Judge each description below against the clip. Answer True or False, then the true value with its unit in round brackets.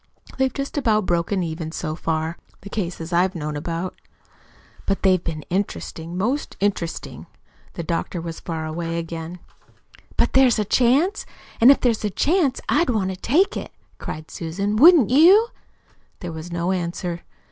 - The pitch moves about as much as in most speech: False (6.0 semitones)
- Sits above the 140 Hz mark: True (185 Hz)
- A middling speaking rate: True (160 wpm)